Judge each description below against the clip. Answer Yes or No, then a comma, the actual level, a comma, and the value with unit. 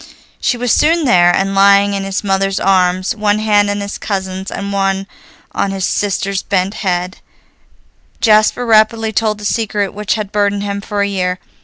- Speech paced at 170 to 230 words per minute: Yes, average, 175 wpm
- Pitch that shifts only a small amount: Yes, narrow, 1.7 semitones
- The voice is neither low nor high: No, high, 200 Hz